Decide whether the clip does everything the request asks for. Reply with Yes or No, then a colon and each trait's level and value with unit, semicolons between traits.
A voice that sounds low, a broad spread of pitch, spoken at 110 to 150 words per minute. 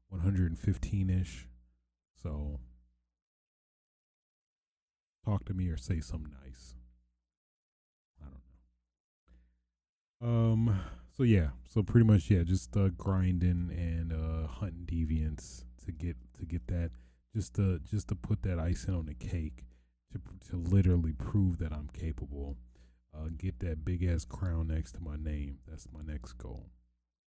Yes: very low, 80 Hz; wide, 6.9 semitones; slow, 135 wpm